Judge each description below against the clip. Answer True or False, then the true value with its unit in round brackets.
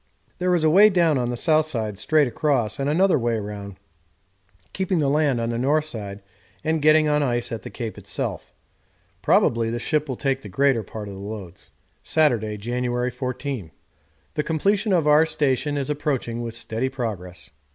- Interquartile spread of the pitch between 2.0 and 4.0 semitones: False (5.1 semitones)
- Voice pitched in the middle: False (130 Hz)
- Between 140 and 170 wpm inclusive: False (185 wpm)